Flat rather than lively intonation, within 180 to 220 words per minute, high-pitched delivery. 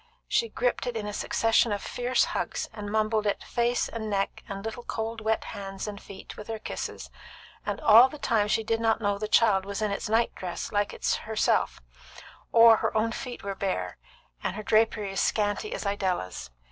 Yes: narrow, 2.0 semitones; average, 200 wpm; high, 215 Hz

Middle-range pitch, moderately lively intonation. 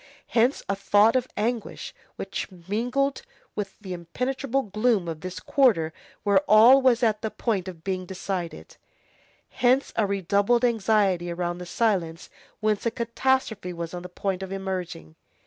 No: high, 200 Hz; average, 4.4 semitones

